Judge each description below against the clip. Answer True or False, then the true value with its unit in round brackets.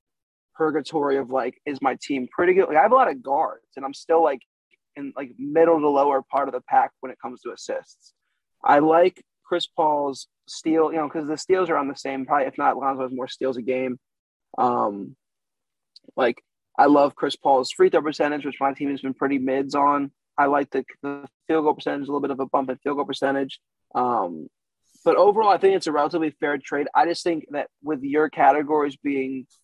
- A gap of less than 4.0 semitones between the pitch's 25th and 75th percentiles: True (2.7 semitones)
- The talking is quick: True (220 wpm)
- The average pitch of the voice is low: False (145 Hz)